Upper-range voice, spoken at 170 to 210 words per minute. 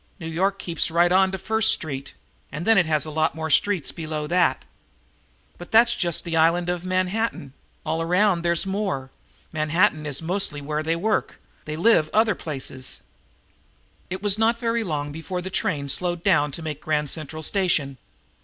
No: medium, 170 Hz; average, 180 wpm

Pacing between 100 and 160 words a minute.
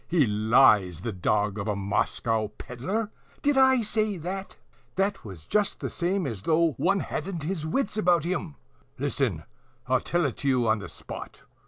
No: average, 170 wpm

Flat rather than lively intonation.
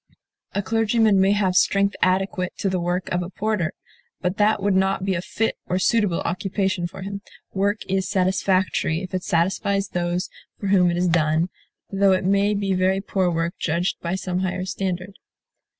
Yes: narrow, 1.8 semitones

